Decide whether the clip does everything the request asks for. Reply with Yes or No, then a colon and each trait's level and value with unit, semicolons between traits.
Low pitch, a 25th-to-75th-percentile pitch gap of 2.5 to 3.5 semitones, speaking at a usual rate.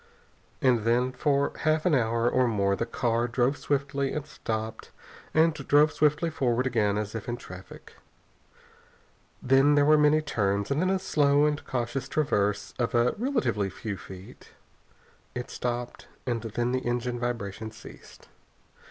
No: low, 125 Hz; average, 4.2 semitones; average, 150 wpm